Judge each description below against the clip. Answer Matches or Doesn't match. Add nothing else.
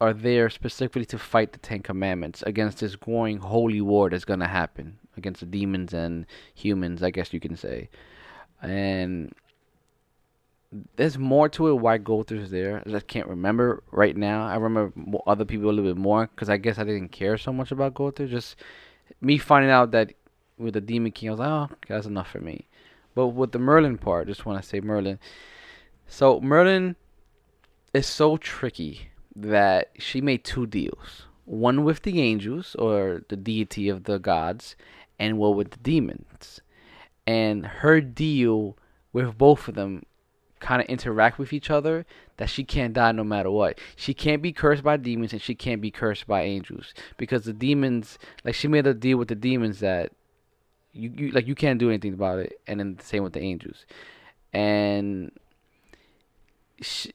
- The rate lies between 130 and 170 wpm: Doesn't match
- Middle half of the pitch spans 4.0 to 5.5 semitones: Matches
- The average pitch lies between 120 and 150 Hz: Doesn't match